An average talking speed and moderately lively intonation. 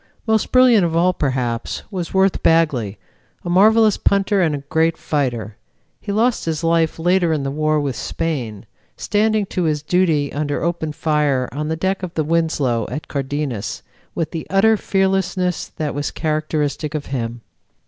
Yes: average, 160 wpm; average, 4.3 semitones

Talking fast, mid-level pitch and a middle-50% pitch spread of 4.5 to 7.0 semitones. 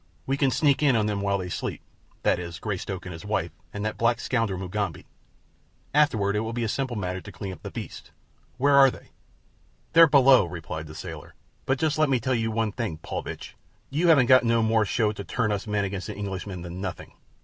No: fast, 210 wpm; low, 105 Hz; average, 5.1 semitones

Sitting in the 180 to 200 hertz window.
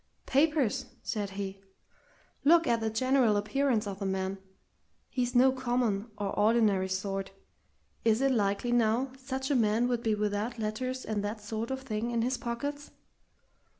No: high, 230 Hz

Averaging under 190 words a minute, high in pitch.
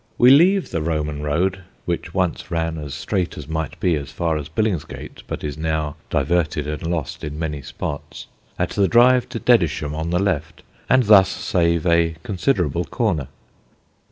No: average, 170 wpm; very low, 80 Hz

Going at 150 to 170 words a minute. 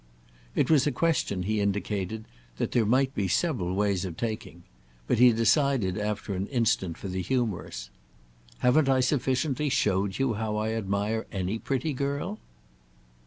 Yes: average, 155 wpm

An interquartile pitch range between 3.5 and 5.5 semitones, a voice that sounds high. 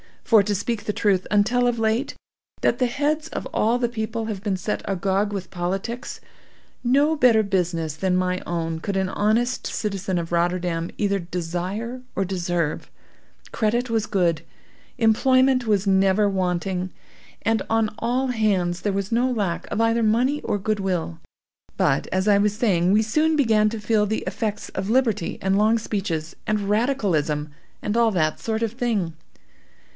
Yes: average, 3.8 semitones; high, 210 Hz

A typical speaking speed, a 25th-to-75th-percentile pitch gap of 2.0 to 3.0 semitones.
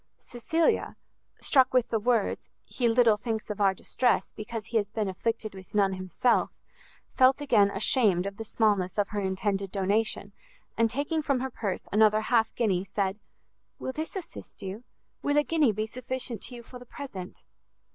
No: average, 175 wpm; average, 3.9 semitones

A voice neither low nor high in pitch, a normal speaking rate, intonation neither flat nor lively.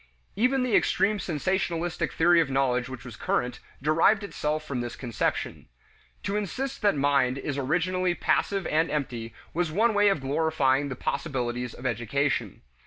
No: medium, 150 Hz; average, 155 wpm; wide, 6.0 semitones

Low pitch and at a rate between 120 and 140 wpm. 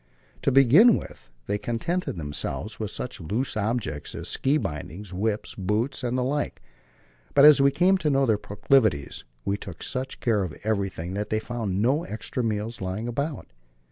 No: low, 110 Hz; average, 175 wpm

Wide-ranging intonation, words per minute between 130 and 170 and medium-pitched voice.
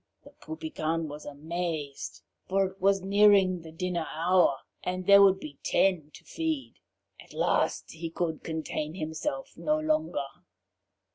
No: average, 3.8 semitones; average, 140 wpm; medium, 180 Hz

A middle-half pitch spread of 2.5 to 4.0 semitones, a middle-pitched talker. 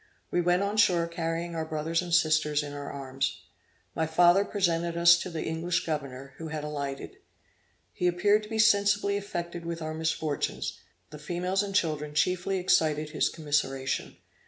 Yes: average, 2.9 semitones; medium, 165 Hz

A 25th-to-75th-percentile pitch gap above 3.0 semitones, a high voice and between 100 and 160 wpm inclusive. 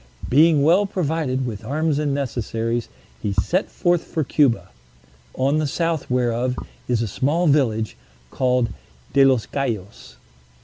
No: average, 4.5 semitones; low, 135 Hz; slow, 135 wpm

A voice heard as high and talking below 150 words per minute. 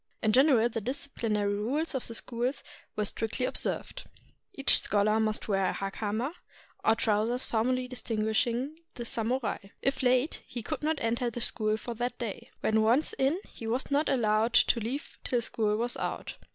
No: high, 235 Hz; average, 170 wpm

